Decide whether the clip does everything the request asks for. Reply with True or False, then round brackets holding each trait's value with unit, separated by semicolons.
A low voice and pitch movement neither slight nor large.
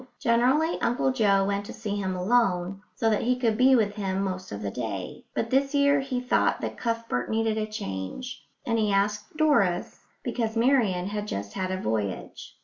False (215 Hz; 4.6 semitones)